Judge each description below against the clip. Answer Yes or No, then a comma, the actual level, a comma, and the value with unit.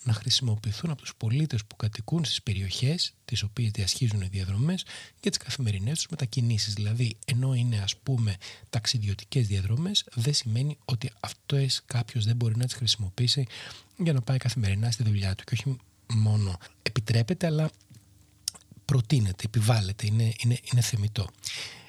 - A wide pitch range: No, average, 3.6 semitones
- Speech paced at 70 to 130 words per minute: No, average, 150 wpm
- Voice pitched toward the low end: Yes, low, 115 Hz